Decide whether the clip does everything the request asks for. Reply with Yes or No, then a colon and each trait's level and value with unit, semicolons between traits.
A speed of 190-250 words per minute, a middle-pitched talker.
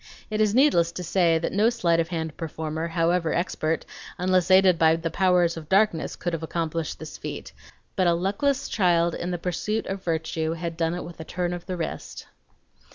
Yes: average, 200 wpm; medium, 170 Hz